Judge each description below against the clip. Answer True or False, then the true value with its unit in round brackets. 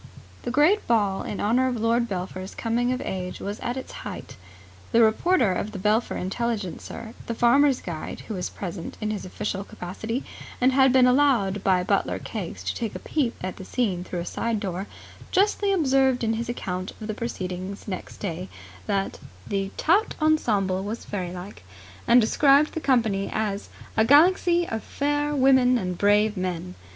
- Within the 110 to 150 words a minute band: False (175 wpm)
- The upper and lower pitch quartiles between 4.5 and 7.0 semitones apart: True (5.2 semitones)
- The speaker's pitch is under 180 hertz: False (220 Hz)